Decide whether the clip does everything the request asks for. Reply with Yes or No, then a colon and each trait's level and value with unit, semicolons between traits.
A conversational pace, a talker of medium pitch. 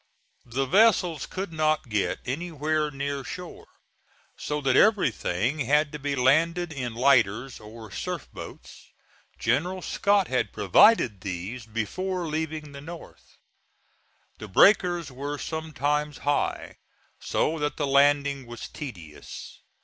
No: slow, 120 wpm; medium, 145 Hz